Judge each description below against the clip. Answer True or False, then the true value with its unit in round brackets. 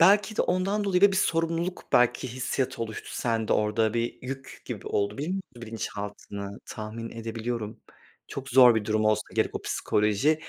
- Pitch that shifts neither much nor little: False (7.0 semitones)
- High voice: False (120 Hz)